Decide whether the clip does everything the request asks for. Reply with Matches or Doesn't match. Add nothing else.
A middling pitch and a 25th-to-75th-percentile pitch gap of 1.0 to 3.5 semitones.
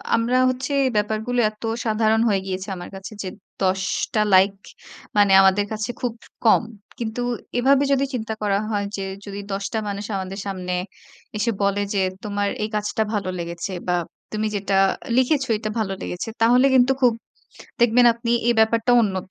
Doesn't match